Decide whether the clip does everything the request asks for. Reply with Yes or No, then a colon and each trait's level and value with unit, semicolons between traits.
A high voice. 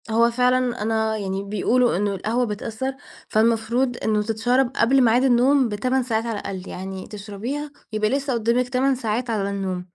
Yes: high, 230 Hz